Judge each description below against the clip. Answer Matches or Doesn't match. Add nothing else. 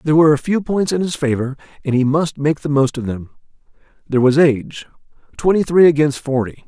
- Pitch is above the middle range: Doesn't match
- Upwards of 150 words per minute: Matches